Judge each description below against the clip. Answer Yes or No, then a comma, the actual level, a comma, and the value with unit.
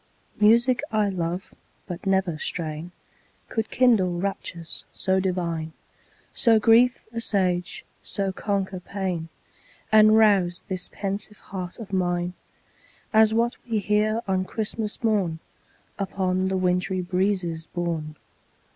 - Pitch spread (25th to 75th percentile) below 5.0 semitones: Yes, average, 3.2 semitones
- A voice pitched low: No, high, 190 Hz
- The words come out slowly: Yes, slow, 115 wpm